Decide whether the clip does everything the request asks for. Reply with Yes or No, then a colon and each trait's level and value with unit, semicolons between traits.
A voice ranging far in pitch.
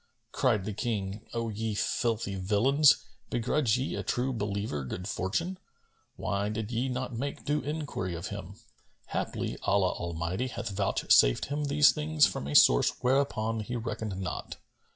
No: average, 5.0 semitones